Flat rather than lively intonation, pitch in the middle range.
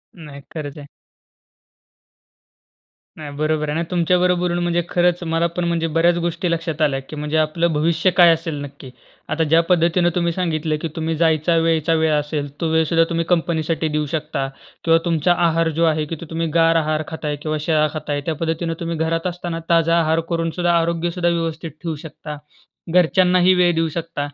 Yes: narrow, 1.6 semitones; medium, 165 Hz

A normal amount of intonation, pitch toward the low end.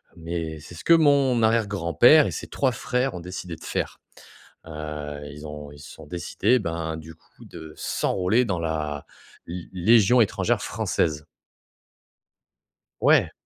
No: wide, 6.7 semitones; very low, 85 Hz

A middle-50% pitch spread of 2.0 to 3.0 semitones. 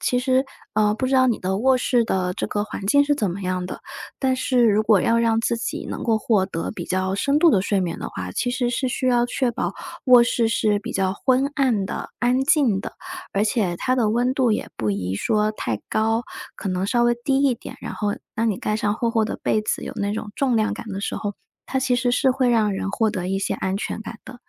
No: average, 4.0 semitones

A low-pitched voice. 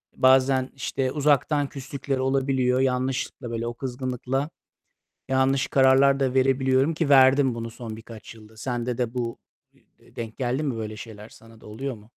Yes: low, 130 Hz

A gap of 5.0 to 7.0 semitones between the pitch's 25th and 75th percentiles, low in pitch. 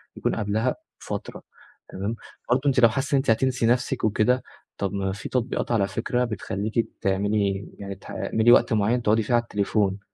No: average, 3.3 semitones; low, 110 Hz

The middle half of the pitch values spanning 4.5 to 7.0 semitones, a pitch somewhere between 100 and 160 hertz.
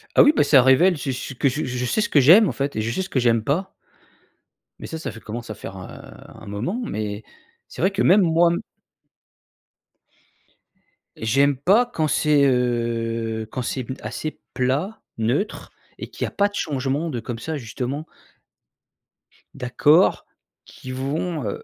Yes: wide, 5.4 semitones; low, 135 Hz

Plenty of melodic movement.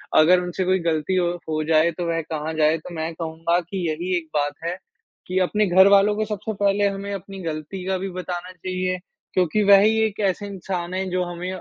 No: average, 2.8 semitones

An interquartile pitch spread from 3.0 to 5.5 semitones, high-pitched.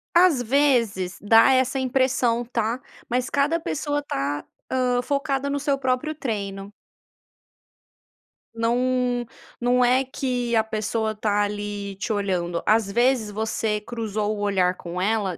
Yes: average, 3.9 semitones; high, 230 Hz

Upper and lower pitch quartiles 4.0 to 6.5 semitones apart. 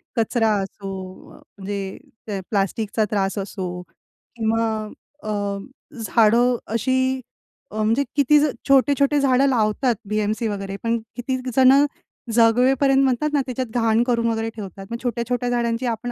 No: average, 3.3 semitones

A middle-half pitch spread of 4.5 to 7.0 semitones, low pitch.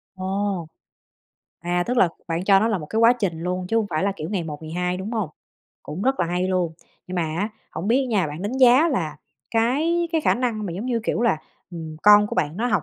No: average, 4.9 semitones; high, 195 Hz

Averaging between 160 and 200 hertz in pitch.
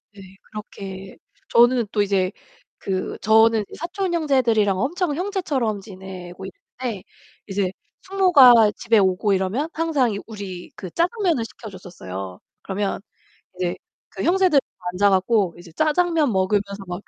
No: high, 210 Hz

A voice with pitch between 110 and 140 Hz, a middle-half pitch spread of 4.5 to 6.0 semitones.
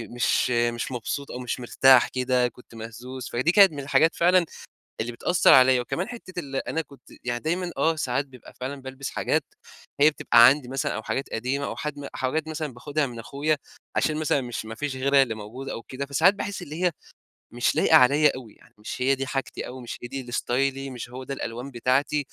No: low, 135 Hz; average, 3.3 semitones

